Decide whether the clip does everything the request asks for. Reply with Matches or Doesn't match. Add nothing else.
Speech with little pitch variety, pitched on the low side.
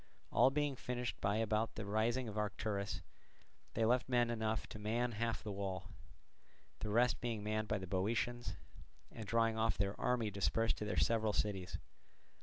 Matches